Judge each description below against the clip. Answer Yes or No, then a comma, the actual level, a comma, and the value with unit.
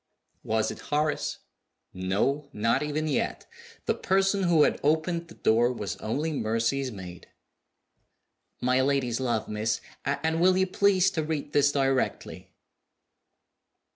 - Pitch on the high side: No, medium, 140 Hz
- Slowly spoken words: Yes, slow, 130 wpm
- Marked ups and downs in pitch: Yes, wide, 5.7 semitones